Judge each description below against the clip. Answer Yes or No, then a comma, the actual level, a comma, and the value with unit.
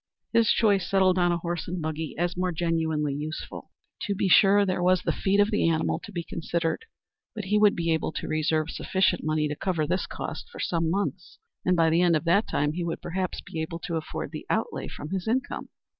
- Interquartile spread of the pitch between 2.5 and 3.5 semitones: Yes, average, 2.9 semitones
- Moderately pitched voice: Yes, medium, 175 Hz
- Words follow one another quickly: Yes, fast, 225 wpm